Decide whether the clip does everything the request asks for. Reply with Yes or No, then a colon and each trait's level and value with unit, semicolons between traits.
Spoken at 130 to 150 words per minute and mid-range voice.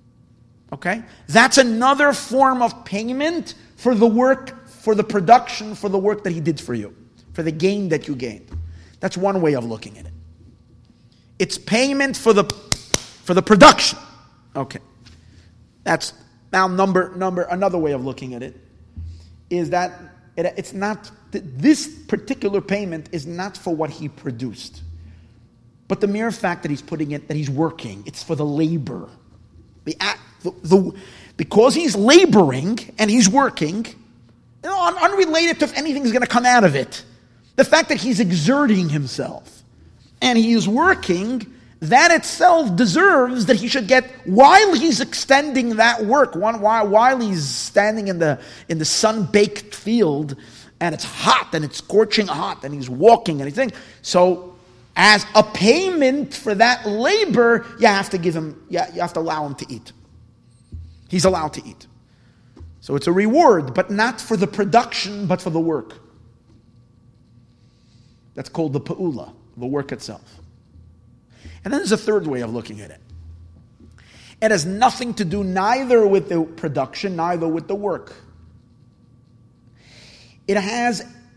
No: average, 160 wpm; medium, 180 Hz